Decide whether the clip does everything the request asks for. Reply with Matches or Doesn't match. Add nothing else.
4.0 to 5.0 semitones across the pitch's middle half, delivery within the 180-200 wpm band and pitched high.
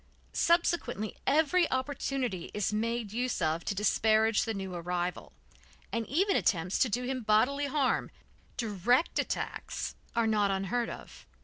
Doesn't match